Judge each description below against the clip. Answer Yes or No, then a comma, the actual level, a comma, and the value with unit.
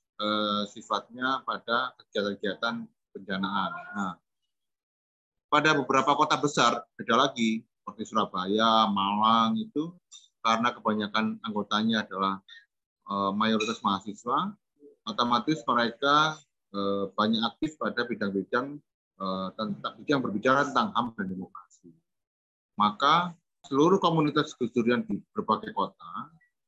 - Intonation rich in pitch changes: Yes, wide, 6.2 semitones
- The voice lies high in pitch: No, low, 115 Hz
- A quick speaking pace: No, average, 90 wpm